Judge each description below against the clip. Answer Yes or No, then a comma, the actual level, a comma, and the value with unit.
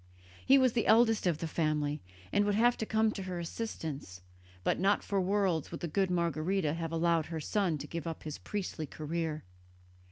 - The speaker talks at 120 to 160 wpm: No, average, 190 wpm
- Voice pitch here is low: No, medium, 170 Hz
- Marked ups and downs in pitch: No, average, 4.4 semitones